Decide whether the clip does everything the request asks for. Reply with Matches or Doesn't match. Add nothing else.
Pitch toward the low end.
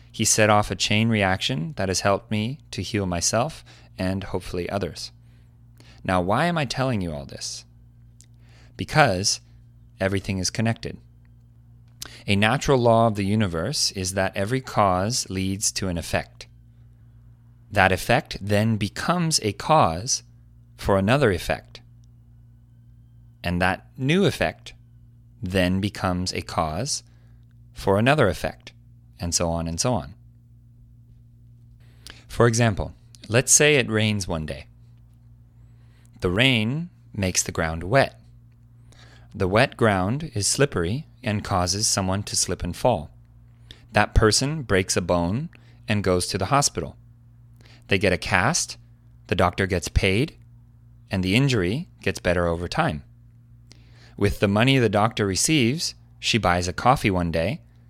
Matches